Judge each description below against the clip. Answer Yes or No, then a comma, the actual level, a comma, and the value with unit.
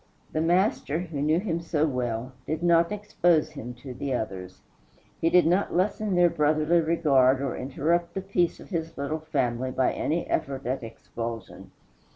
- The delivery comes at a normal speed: Yes, average, 170 wpm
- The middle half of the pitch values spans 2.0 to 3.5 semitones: No, average, 4.8 semitones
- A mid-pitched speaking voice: Yes, medium, 155 Hz